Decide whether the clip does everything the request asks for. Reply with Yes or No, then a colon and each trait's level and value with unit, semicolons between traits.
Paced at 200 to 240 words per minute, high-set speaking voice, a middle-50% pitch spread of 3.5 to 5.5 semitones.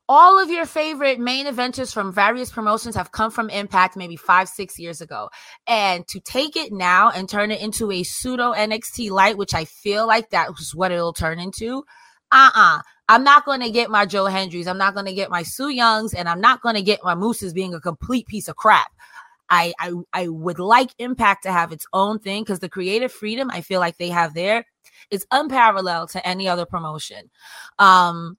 Yes: fast, 205 wpm; high, 200 Hz; average, 4.5 semitones